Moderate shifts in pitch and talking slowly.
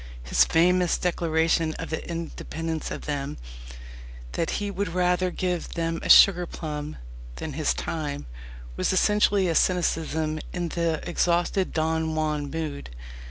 No: narrow, 2.2 semitones; slow, 130 wpm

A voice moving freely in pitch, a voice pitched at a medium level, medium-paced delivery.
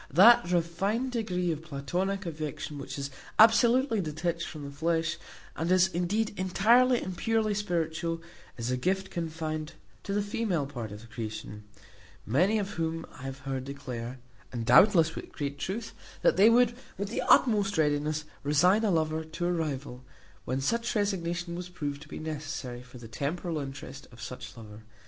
Yes: wide, 5.7 semitones; medium, 165 Hz; average, 170 wpm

